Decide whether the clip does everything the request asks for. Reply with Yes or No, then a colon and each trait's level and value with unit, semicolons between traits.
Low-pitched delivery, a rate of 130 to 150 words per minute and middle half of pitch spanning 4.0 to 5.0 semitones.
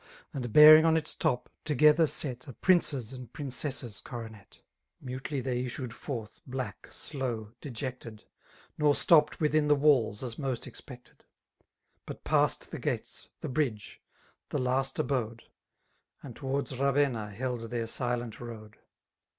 No: low, 130 Hz; slow, 135 wpm; average, 3.4 semitones